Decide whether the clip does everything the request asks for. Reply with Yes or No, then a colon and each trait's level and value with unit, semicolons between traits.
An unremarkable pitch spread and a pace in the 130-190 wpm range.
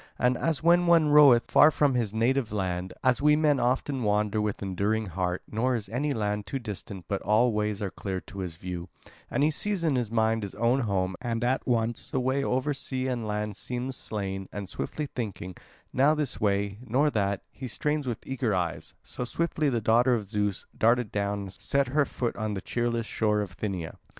No: average, 4.5 semitones; fast, 205 wpm